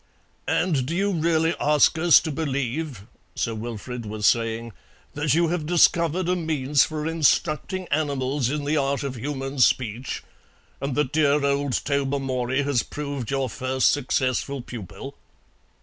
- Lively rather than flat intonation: No, average, 3.3 semitones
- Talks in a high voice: No, medium, 140 Hz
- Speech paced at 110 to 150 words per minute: Yes, average, 145 wpm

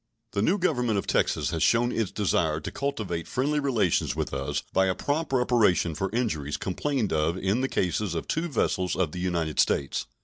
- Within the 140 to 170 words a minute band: No, average, 195 wpm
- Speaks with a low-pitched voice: Yes, low, 100 Hz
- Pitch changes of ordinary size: No, wide, 6.7 semitones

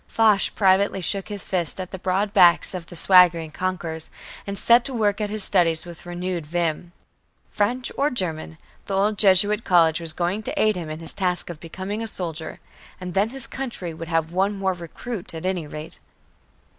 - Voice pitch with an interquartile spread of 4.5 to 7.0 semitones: No, average, 3.4 semitones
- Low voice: No, medium, 185 Hz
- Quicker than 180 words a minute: Yes, average, 195 wpm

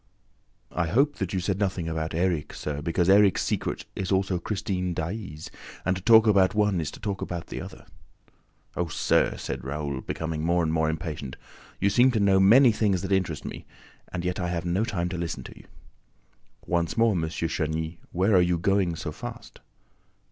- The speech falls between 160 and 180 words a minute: No, average, 200 wpm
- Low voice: Yes, very low, 90 Hz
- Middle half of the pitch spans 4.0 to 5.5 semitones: No, average, 3.2 semitones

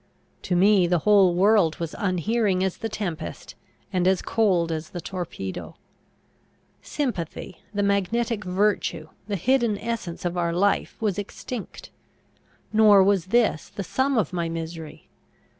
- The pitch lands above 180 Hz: Yes, high, 190 Hz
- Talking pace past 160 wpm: No, average, 140 wpm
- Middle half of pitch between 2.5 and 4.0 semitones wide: Yes, average, 3.6 semitones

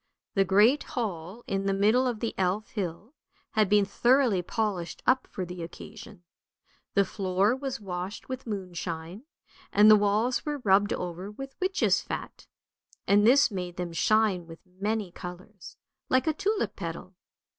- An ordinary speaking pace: Yes, average, 155 wpm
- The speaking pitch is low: No, high, 205 Hz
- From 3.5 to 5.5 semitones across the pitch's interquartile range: Yes, average, 4.4 semitones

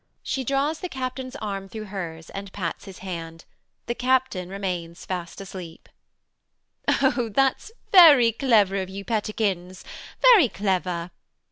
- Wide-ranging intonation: Yes, wide, 5.8 semitones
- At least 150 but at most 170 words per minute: No, average, 140 wpm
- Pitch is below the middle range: No, high, 200 Hz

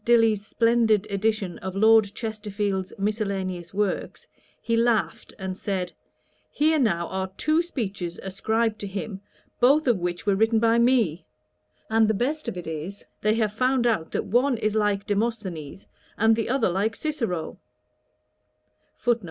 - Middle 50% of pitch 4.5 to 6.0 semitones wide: No, average, 3.2 semitones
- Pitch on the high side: Yes, high, 215 Hz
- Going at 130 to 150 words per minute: Yes, average, 145 wpm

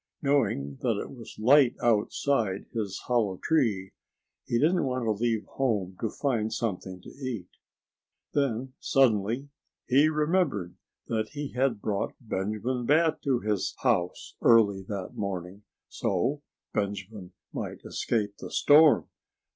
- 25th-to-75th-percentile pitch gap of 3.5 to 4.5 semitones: No, average, 5.2 semitones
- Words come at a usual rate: No, slow, 130 wpm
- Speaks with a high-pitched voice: No, low, 115 Hz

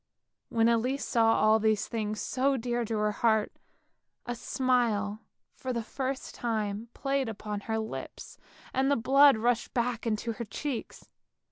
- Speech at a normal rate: Yes, average, 150 wpm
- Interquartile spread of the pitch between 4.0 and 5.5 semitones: No, average, 2.7 semitones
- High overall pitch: Yes, high, 230 Hz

